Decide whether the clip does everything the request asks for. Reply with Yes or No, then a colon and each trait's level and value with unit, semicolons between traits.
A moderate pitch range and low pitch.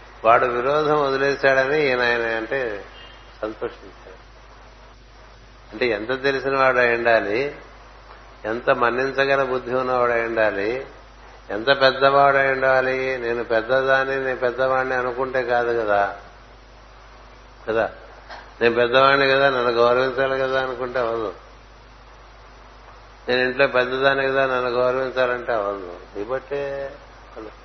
No: narrow, 2.0 semitones; low, 130 Hz